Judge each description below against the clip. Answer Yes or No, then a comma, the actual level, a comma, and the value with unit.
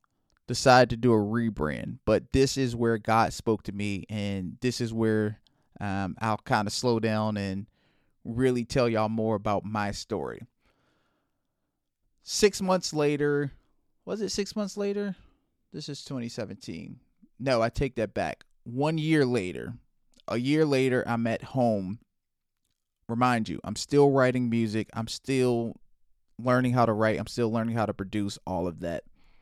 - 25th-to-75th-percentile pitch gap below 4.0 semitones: Yes, average, 3.6 semitones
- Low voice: Yes, low, 115 Hz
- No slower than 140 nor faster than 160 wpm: Yes, average, 155 wpm